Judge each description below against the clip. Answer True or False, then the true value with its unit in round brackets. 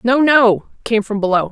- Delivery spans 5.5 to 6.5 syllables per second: False (4.7 syllables/s)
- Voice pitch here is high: True (225 Hz)